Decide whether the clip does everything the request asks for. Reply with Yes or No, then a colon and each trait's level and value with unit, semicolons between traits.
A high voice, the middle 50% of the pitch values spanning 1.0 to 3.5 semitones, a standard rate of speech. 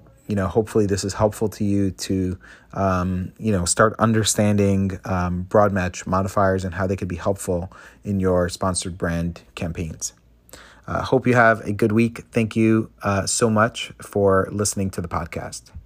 No: low, 100 Hz; average, 2.8 semitones; average, 180 wpm